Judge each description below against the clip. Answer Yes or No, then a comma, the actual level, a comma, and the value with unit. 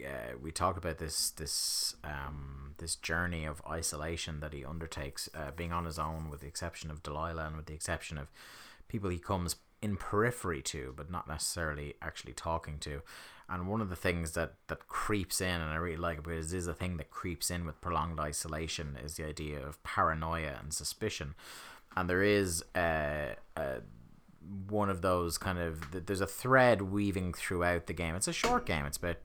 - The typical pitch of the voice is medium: No, very low, 85 Hz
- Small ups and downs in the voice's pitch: No, average, 3.1 semitones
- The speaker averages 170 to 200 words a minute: Yes, average, 195 wpm